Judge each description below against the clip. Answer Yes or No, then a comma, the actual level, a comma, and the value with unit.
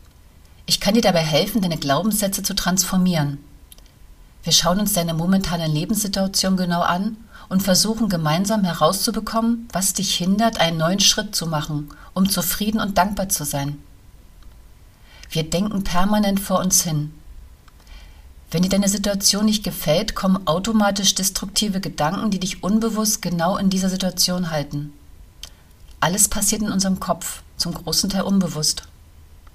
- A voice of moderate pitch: Yes, medium, 180 Hz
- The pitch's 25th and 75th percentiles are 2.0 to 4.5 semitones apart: No, average, 4.9 semitones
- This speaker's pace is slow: No, average, 140 wpm